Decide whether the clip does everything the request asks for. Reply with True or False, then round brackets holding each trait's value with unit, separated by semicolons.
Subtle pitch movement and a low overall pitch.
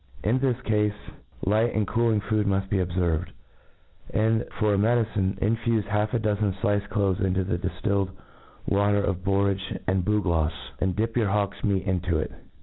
True (2.3 semitones; 100 Hz)